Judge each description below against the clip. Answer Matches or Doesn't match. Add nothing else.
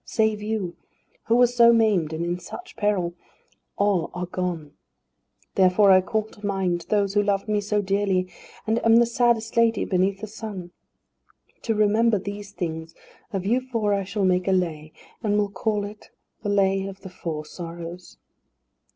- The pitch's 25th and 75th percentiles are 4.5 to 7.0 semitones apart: Doesn't match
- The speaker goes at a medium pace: Matches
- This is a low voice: Doesn't match